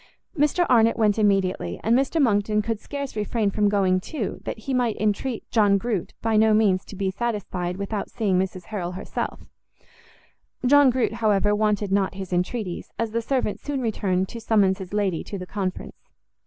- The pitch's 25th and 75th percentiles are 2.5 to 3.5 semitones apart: Yes, average, 3.1 semitones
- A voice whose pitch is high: Yes, high, 210 Hz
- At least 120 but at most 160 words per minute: No, average, 180 wpm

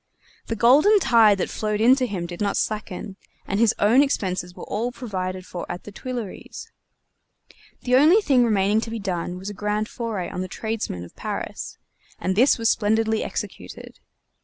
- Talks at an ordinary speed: Yes, average, 180 wpm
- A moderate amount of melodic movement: Yes, average, 3.8 semitones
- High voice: Yes, high, 215 Hz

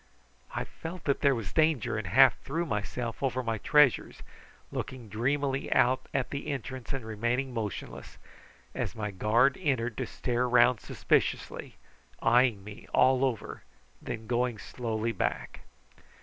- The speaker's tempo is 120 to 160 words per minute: Yes, average, 145 wpm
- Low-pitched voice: Yes, low, 125 Hz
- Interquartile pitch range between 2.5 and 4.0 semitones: Yes, average, 3.2 semitones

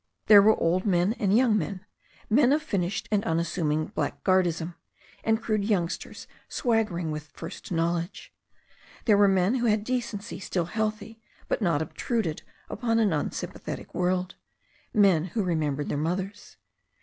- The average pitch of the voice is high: Yes, high, 195 Hz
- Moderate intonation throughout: Yes, average, 4.3 semitones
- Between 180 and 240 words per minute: No, average, 145 wpm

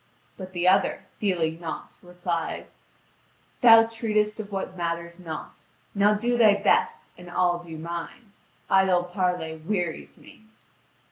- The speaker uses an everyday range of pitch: Yes, average, 3.4 semitones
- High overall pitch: No, medium, 180 Hz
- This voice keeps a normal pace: No, slow, 130 wpm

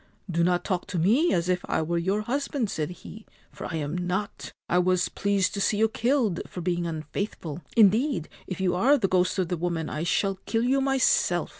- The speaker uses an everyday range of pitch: Yes, average, 4.0 semitones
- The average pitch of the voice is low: No, medium, 185 Hz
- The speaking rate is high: Yes, fast, 225 wpm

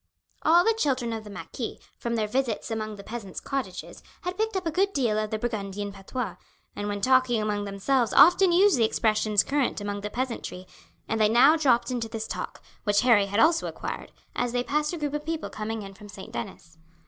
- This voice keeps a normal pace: No, fast, 210 wpm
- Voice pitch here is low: No, high, 230 Hz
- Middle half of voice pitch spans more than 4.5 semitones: Yes, average, 5.3 semitones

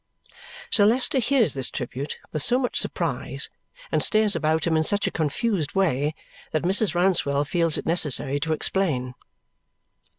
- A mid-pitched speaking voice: Yes, medium, 165 Hz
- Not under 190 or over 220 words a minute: No, average, 155 wpm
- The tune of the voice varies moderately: No, wide, 5.8 semitones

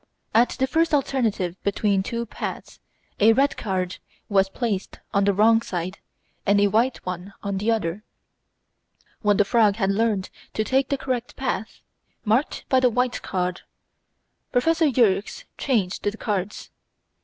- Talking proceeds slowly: No, average, 150 wpm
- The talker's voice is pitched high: Yes, high, 215 Hz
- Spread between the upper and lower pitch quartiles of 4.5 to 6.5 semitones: No, average, 4.1 semitones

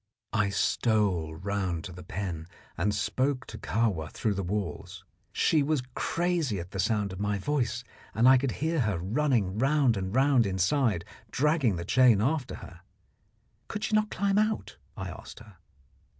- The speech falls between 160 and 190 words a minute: Yes, average, 165 wpm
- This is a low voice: Yes, low, 110 Hz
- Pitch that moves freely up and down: Yes, wide, 6.3 semitones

